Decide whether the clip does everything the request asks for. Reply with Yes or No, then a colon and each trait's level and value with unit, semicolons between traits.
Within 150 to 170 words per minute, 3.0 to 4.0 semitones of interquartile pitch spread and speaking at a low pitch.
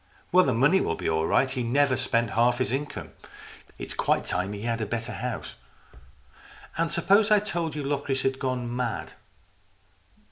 No: average, 185 wpm; average, 3.7 semitones; low, 130 Hz